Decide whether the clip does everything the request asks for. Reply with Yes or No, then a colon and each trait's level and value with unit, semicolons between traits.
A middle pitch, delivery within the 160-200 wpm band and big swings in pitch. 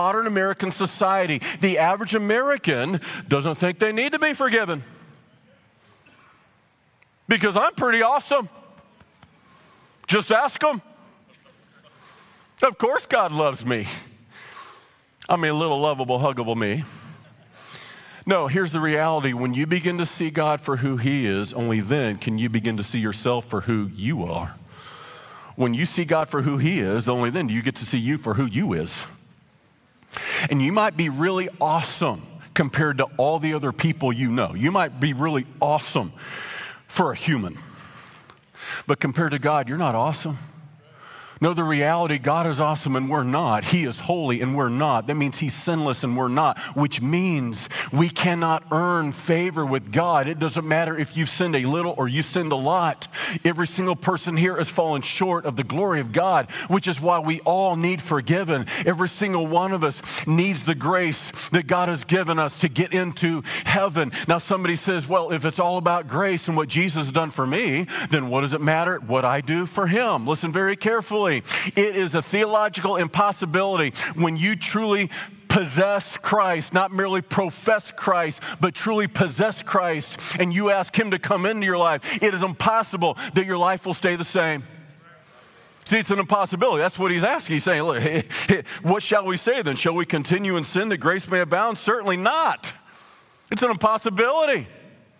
No: medium, 170 Hz; average, 180 wpm; average, 4.3 semitones